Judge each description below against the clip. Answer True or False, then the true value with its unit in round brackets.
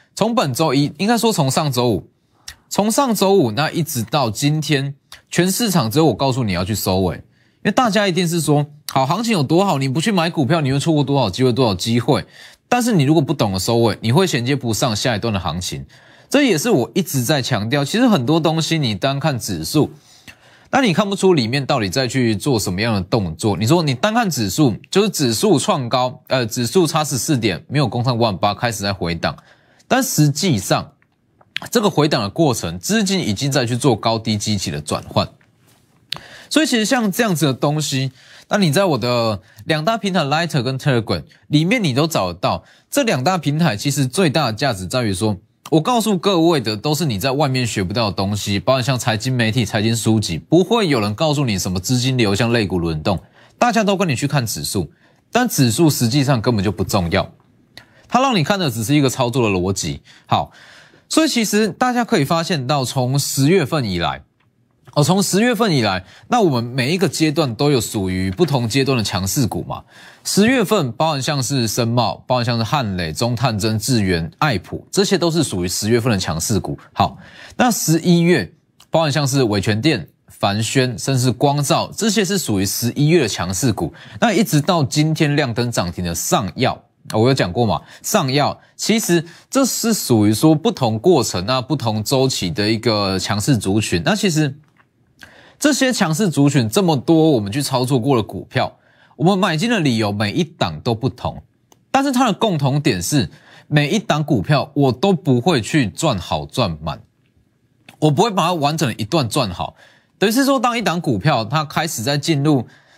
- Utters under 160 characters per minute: False (295 characters per minute)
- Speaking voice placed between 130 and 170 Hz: True (140 Hz)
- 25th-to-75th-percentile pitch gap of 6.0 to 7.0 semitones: True (6.5 semitones)